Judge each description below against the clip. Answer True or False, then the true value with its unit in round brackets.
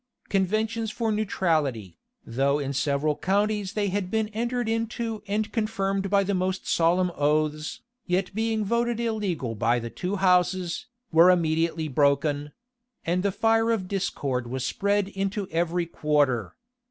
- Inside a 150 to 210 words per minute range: False (140 wpm)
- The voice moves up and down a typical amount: False (5.7 semitones)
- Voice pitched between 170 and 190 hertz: True (185 Hz)